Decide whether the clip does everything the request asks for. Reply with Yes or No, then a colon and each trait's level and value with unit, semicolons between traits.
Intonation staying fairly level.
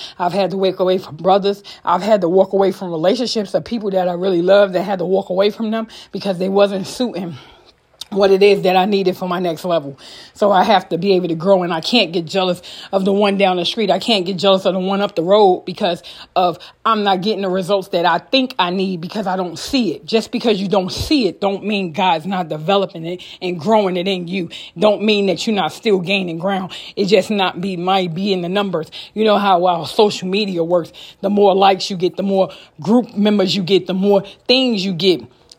Yes: narrow, 1.9 semitones